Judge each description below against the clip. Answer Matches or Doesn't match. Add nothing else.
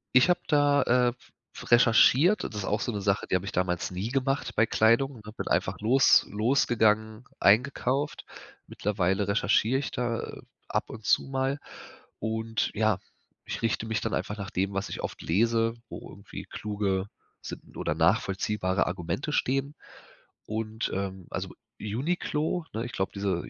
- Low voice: Matches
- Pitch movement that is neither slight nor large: Matches